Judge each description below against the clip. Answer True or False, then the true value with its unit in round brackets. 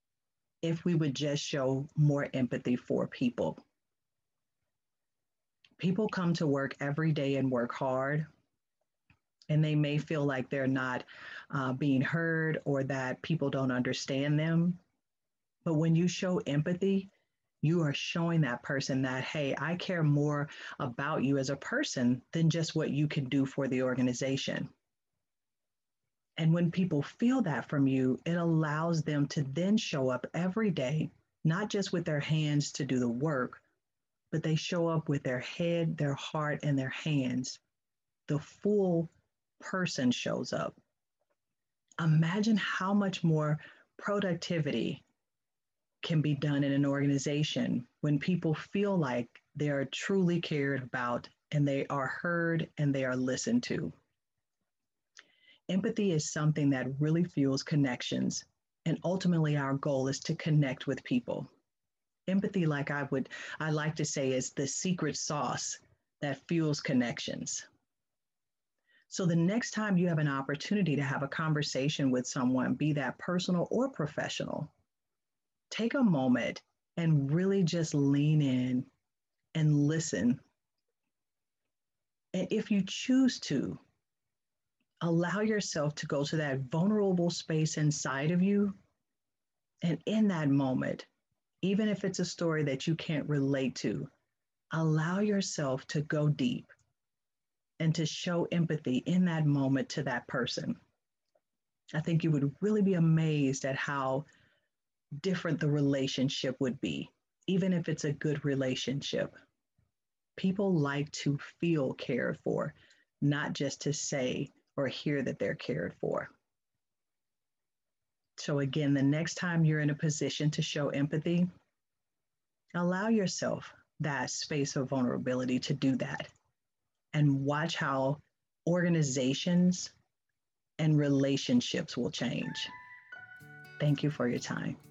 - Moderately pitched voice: True (150 Hz)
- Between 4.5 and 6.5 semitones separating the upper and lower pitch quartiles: False (3.8 semitones)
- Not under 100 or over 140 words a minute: True (135 wpm)